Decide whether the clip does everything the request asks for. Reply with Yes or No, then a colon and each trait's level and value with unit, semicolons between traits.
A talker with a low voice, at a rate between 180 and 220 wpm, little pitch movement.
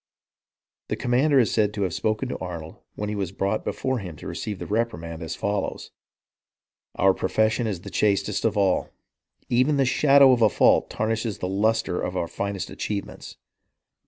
No: low, 105 Hz; average, 190 wpm; average, 3.4 semitones